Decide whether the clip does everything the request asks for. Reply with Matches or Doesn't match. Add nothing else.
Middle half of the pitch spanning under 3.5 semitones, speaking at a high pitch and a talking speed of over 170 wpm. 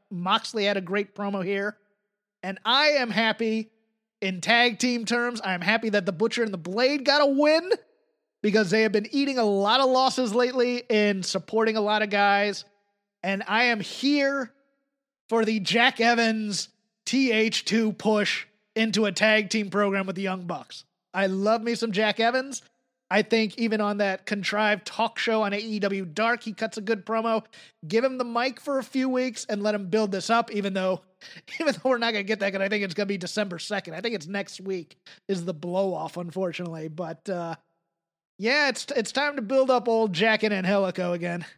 Matches